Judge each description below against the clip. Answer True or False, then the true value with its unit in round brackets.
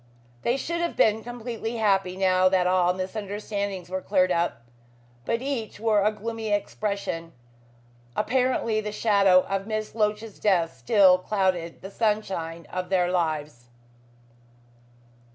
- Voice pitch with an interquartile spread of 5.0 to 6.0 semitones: False (2.9 semitones)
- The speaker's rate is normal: False (130 wpm)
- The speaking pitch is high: True (200 Hz)